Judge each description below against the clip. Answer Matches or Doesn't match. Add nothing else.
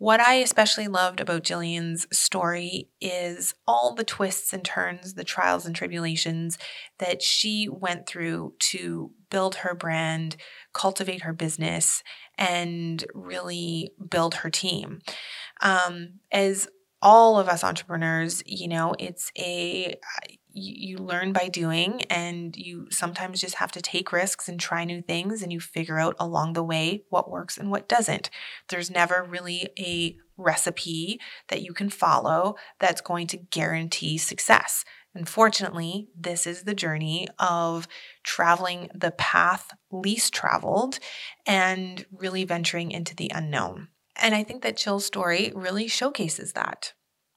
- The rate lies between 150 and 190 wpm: Doesn't match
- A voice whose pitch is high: Doesn't match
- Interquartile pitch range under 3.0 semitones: Matches